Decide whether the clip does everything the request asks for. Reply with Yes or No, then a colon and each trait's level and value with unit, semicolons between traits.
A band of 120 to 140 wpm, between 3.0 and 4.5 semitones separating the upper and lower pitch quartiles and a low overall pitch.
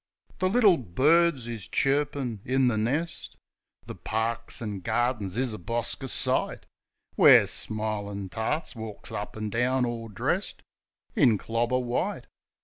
Yes: slow, 135 wpm; average, 3.5 semitones; low, 120 Hz